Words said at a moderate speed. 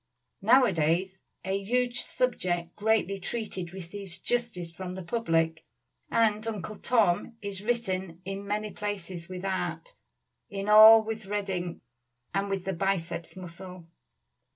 No: slow, 130 wpm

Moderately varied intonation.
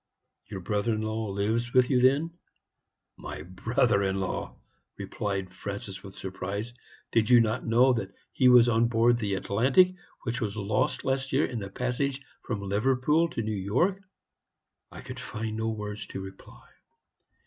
Yes: average, 3.8 semitones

